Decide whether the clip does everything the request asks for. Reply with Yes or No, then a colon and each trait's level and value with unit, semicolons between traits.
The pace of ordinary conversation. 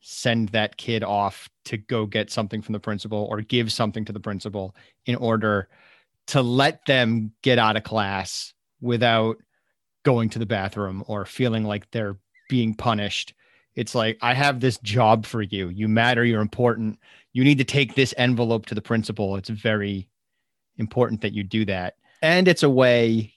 Yes: average, 175 wpm